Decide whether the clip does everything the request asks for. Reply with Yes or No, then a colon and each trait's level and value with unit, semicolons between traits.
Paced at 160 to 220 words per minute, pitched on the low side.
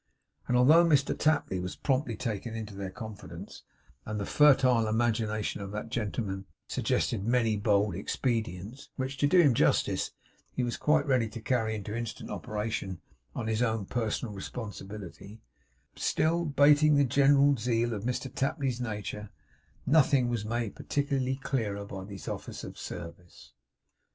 No: average, 145 wpm; low, 115 Hz